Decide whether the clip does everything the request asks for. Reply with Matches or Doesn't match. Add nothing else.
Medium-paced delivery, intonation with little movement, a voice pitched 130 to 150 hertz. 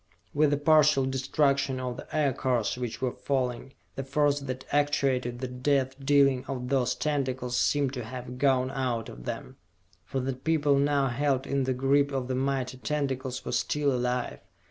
Matches